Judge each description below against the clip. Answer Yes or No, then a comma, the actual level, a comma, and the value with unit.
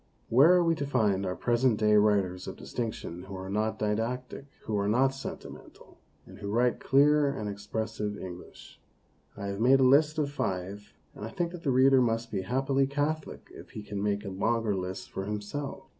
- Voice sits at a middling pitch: No, low, 110 Hz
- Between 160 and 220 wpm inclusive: Yes, average, 195 wpm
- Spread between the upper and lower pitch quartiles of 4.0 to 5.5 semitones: Yes, average, 5.0 semitones